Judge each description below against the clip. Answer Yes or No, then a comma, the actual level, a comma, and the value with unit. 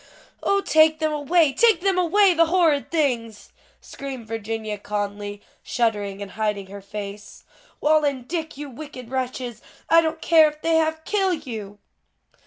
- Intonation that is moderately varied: No, wide, 6.8 semitones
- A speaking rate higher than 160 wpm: No, average, 155 wpm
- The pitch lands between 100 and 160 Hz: No, very high, 280 Hz